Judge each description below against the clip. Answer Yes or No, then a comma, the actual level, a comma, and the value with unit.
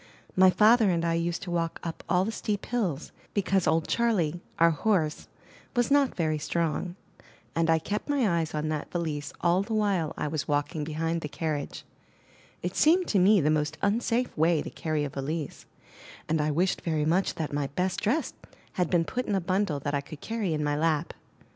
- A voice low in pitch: No, medium, 170 Hz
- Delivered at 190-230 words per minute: Yes, average, 200 wpm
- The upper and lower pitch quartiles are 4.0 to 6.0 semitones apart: Yes, average, 4.3 semitones